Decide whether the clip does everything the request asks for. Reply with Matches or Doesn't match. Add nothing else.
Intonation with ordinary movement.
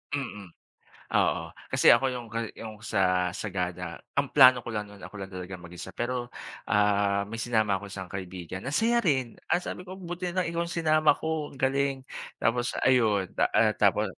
Doesn't match